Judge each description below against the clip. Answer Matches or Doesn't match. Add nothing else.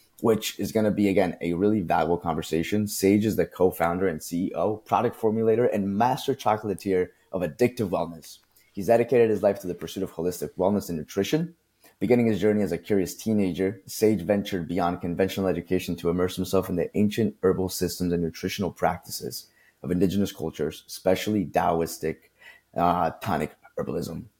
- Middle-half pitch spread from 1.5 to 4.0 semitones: Matches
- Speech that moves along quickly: Doesn't match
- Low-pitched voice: Matches